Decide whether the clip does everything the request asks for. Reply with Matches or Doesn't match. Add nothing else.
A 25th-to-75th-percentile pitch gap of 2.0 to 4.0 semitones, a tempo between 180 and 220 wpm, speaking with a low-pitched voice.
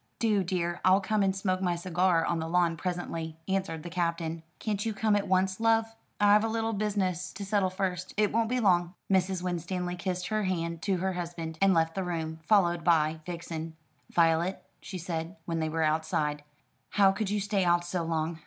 Doesn't match